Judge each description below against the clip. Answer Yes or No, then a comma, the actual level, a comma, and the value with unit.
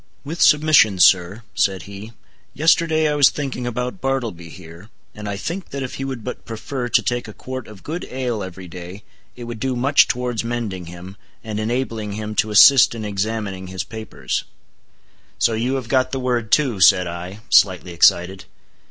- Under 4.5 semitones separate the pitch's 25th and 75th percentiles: No, average, 5.1 semitones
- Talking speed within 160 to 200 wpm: Yes, average, 180 wpm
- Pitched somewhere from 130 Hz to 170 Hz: No, low, 110 Hz